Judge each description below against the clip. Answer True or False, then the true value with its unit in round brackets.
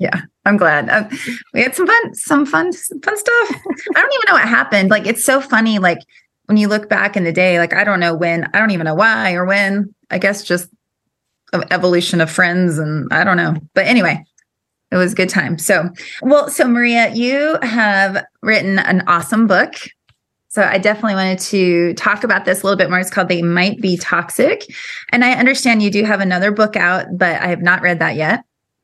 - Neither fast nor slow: False (215 wpm)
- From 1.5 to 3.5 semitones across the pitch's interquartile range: False (4.2 semitones)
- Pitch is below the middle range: False (195 Hz)